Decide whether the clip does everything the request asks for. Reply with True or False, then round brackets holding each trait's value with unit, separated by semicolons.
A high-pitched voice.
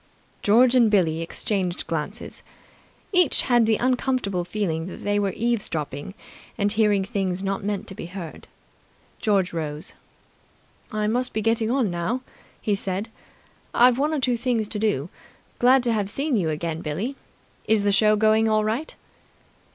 True (210 Hz)